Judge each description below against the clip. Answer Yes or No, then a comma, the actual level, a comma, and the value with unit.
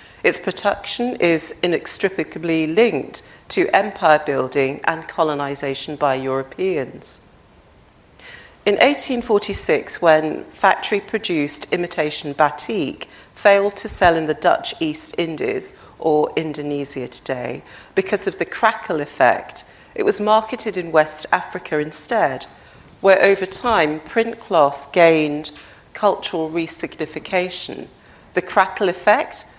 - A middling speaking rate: No, slow, 105 wpm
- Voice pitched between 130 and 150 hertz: No, medium, 175 Hz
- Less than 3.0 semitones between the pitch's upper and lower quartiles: No, average, 5.2 semitones